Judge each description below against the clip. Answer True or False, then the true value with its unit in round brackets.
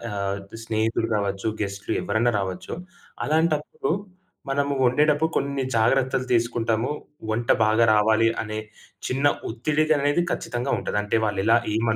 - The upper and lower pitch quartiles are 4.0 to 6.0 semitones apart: True (4.4 semitones)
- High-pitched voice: False (115 Hz)